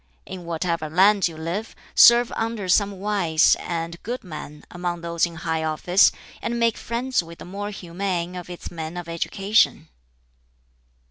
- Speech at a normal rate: Yes, average, 155 wpm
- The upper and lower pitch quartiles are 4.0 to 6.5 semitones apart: No, average, 3.4 semitones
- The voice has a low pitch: No, medium, 180 Hz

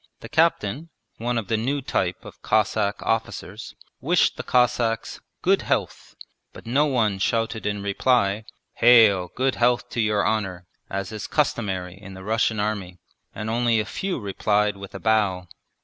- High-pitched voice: No, low, 110 Hz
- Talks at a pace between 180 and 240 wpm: No, average, 160 wpm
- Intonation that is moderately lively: Yes, average, 3.1 semitones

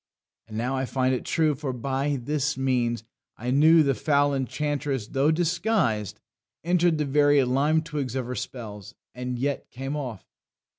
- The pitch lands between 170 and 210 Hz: No, low, 135 Hz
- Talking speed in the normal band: Yes, average, 160 wpm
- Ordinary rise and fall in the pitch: Yes, average, 3.0 semitones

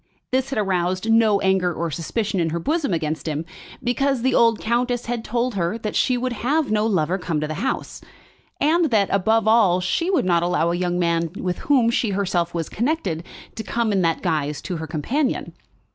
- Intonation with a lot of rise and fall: Yes, wide, 5.8 semitones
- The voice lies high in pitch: Yes, high, 200 Hz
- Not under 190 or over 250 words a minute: Yes, fast, 205 wpm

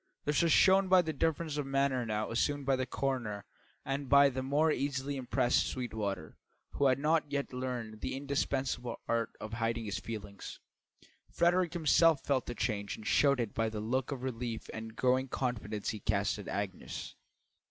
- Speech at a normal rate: Yes, average, 175 wpm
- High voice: No, low, 130 Hz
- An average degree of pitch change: Yes, average, 4.0 semitones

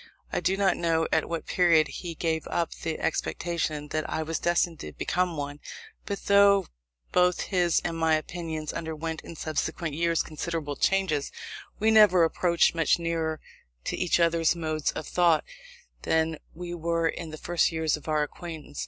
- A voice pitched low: No, medium, 165 Hz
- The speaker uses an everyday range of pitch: No, narrow, 1.7 semitones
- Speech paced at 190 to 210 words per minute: No, average, 170 wpm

